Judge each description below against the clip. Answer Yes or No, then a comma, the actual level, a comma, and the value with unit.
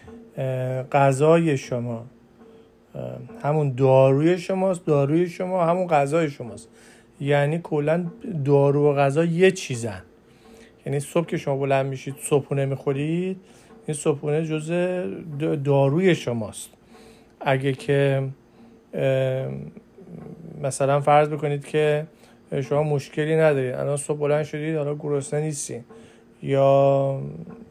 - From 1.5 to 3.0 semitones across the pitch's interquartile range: Yes, average, 2.7 semitones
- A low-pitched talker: No, medium, 145 Hz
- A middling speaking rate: No, slow, 100 wpm